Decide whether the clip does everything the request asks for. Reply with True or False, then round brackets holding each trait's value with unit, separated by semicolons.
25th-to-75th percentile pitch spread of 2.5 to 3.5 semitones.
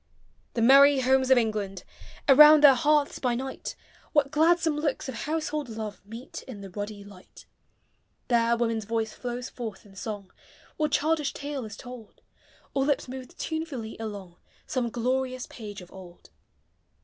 False (4.5 semitones)